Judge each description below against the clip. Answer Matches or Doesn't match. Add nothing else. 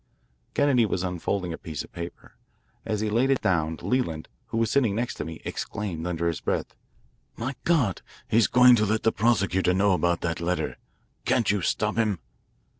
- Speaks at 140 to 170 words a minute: Doesn't match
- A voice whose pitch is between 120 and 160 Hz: Doesn't match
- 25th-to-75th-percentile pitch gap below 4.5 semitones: Doesn't match